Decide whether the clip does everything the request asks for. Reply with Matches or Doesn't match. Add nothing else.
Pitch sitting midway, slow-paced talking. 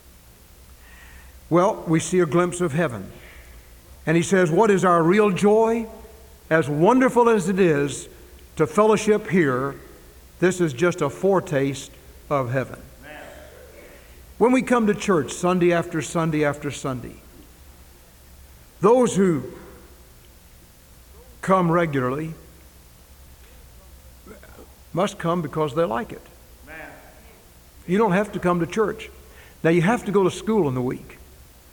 Matches